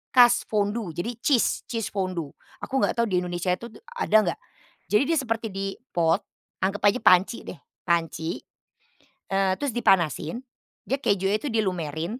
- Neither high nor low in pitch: No, high, 195 Hz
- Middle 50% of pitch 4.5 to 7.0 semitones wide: Yes, average, 4.8 semitones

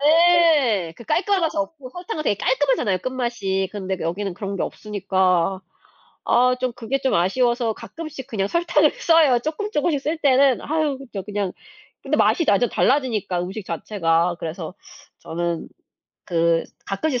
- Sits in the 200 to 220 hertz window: No, high, 235 Hz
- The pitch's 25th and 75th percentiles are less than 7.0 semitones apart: No, wide, 7.3 semitones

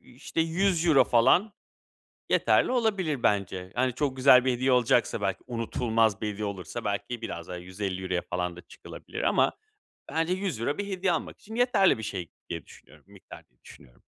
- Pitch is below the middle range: Yes, low, 120 Hz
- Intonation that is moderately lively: No, wide, 8.9 semitones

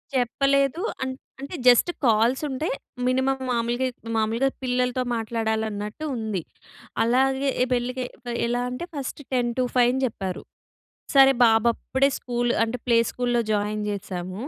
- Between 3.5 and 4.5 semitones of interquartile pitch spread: No, average, 2.8 semitones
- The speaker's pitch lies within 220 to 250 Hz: Yes, high, 245 Hz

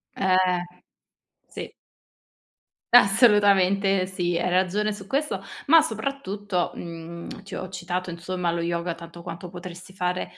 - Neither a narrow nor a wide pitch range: No, narrow, 2.3 semitones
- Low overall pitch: No, medium, 185 Hz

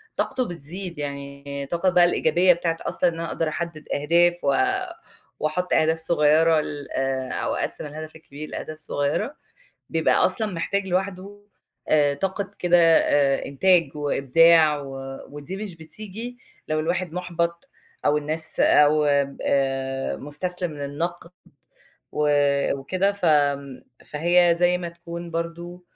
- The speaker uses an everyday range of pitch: Yes, average, 3.3 semitones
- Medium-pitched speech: Yes, medium, 165 Hz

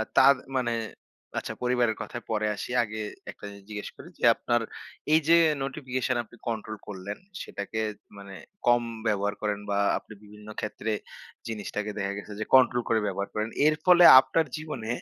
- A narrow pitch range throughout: No, average, 3.3 semitones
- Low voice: Yes, low, 110 Hz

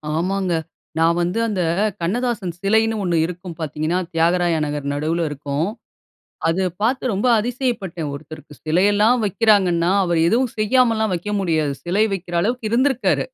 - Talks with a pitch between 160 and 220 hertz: Yes, medium, 185 Hz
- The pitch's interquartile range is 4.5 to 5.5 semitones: Yes, average, 5.0 semitones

